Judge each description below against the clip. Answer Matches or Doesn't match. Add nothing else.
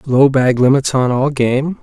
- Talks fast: Doesn't match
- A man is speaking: Matches